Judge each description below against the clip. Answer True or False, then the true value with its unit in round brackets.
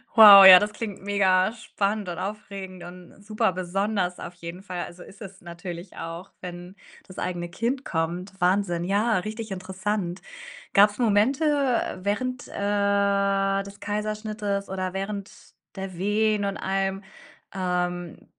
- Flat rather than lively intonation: True (2.3 semitones)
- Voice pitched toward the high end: True (195 Hz)